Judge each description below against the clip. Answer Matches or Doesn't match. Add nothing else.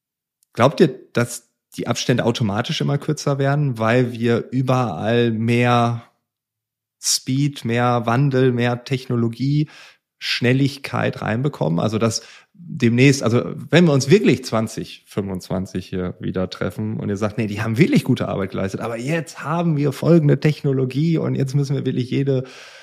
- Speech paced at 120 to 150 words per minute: Matches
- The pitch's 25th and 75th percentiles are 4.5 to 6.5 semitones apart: Doesn't match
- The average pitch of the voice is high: Doesn't match